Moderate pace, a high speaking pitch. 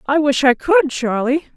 Yes: average, 190 wpm; very high, 260 Hz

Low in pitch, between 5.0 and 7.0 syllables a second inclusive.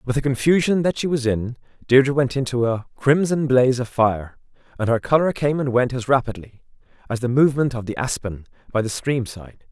Yes: low, 125 Hz; 5.5 syllables/s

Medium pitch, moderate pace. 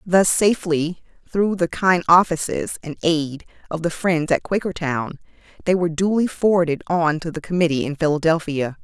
Yes: medium, 165 Hz; average, 155 wpm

